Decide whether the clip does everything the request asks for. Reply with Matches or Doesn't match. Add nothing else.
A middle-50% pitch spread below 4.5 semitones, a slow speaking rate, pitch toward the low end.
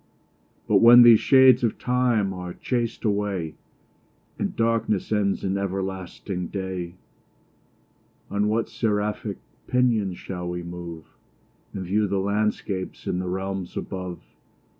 Matches